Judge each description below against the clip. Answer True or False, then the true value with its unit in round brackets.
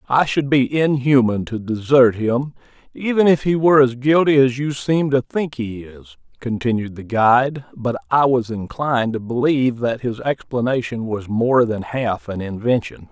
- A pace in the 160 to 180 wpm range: True (175 wpm)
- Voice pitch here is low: True (125 Hz)